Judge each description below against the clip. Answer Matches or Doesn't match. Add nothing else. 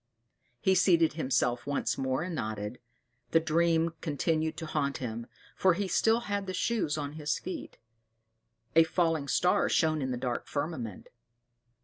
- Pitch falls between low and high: Matches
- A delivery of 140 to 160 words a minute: Matches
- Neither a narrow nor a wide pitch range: Matches